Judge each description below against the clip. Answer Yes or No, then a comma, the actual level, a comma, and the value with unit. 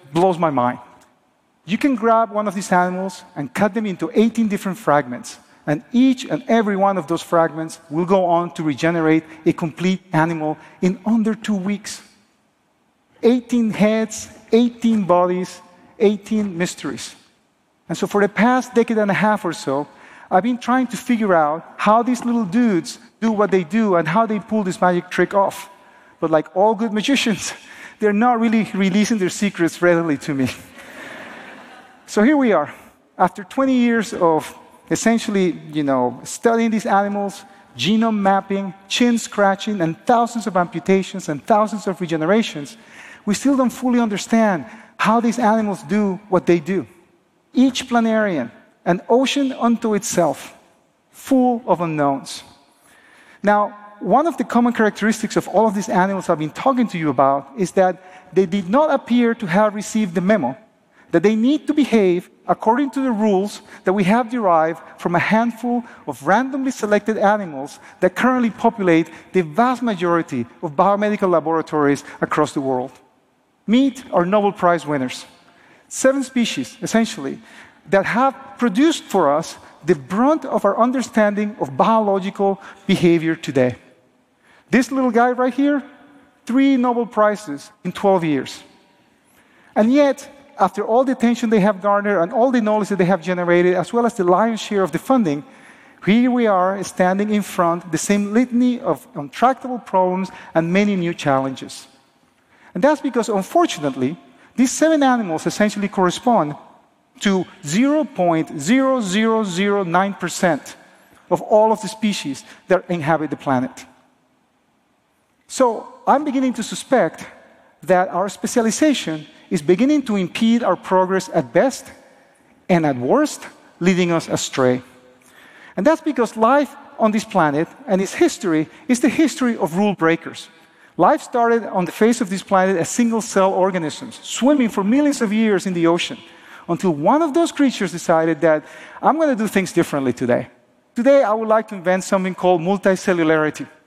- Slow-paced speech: No, average, 155 wpm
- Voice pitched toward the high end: Yes, high, 205 Hz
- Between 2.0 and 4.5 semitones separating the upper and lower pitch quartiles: No, average, 5.2 semitones